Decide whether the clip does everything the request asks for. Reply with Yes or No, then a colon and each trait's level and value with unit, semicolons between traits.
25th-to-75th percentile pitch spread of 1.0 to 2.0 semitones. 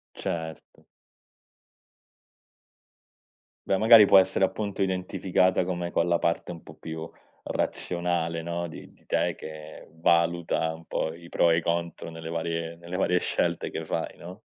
Yes: narrow, 1.5 semitones